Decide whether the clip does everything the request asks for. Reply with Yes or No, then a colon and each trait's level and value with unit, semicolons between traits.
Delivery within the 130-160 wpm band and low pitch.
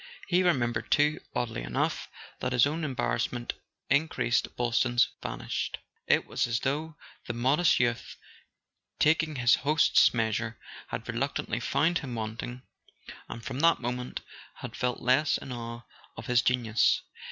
Yes: average, 150 wpm; low, 125 Hz